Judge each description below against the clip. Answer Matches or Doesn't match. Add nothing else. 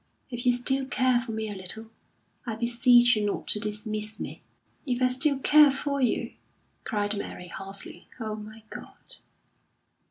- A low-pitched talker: Doesn't match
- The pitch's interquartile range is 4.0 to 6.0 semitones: Doesn't match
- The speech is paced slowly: Doesn't match